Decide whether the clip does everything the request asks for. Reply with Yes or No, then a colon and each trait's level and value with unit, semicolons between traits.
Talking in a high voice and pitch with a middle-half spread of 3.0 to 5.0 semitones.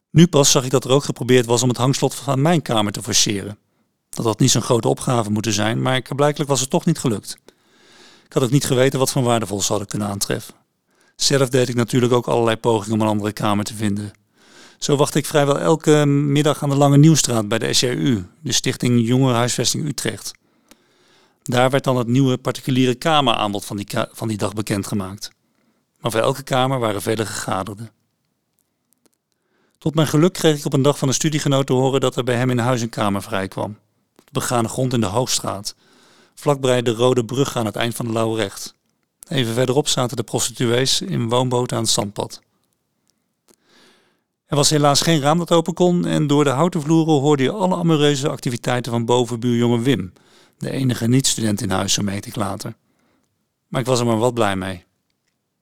No: low, 125 Hz; average, 4.1 semitones